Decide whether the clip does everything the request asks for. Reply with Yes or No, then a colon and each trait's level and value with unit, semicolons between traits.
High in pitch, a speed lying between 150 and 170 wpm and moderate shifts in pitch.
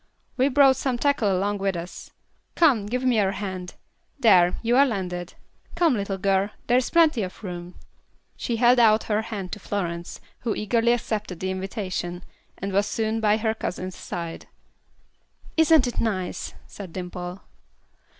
Yes: high, 205 Hz; average, 160 wpm; average, 4.5 semitones